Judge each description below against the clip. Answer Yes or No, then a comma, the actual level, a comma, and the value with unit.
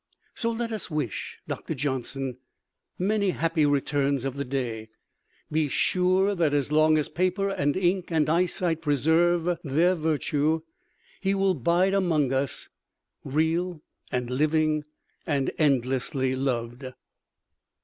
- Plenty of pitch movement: No, average, 4.5 semitones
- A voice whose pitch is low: No, medium, 155 Hz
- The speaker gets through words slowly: Yes, slow, 120 wpm